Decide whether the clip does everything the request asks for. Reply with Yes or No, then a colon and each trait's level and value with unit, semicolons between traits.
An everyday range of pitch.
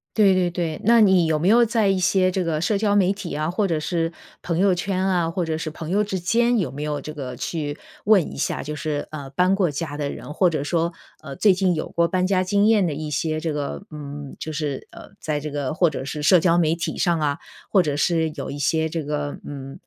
Yes: average, 3.7 semitones